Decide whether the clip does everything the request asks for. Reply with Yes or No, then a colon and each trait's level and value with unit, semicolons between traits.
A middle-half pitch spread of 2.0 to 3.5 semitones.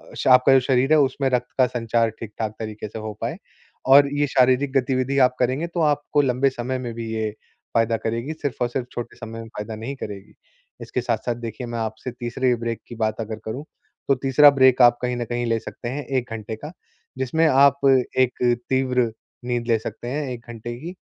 Yes: narrow, 2.6 semitones